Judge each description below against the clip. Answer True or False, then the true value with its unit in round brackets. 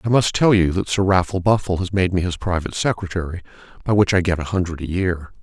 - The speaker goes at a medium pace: False (245 wpm)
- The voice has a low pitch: True (90 Hz)